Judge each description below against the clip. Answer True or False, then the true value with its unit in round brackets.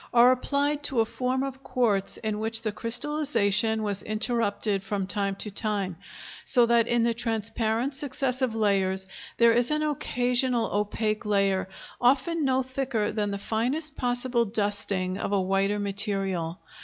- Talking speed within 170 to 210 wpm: False (150 wpm)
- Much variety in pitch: False (3.8 semitones)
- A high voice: True (225 Hz)